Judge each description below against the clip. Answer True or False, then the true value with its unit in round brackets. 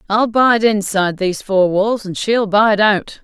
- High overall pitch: True (205 Hz)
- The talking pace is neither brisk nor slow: True (185 wpm)